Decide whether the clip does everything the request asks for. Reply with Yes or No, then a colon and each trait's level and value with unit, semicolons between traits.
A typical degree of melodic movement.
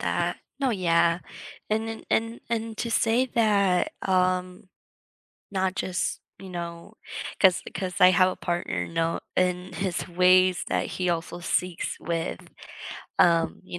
No: narrow, 2.3 semitones